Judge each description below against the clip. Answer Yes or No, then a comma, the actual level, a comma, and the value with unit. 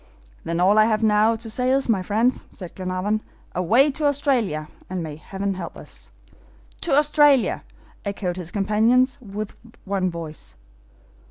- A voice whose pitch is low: No, high, 210 Hz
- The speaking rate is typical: Yes, average, 150 wpm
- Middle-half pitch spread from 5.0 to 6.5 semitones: Yes, average, 5.3 semitones